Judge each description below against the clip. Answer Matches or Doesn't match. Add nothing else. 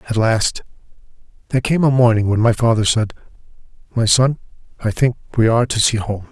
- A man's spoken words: Matches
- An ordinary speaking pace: Matches